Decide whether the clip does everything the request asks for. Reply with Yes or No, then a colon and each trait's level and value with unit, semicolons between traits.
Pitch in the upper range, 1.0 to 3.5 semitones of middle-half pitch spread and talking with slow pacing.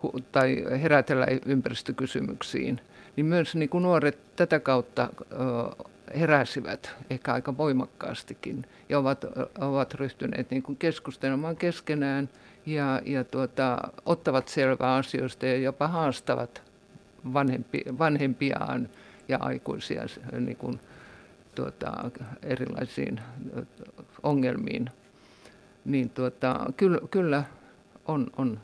No: low, 135 Hz; average, 2.8 semitones; slow, 90 wpm